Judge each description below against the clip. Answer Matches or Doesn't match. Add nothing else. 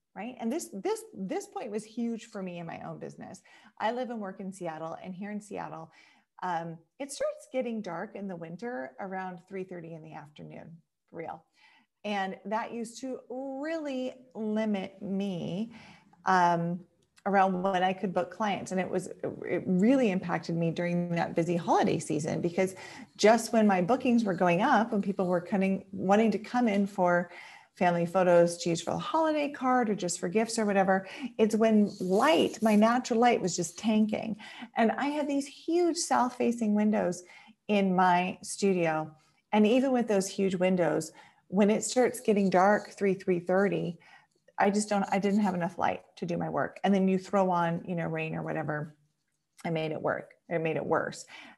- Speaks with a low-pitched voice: Doesn't match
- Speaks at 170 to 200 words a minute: Matches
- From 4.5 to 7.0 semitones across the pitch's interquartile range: Doesn't match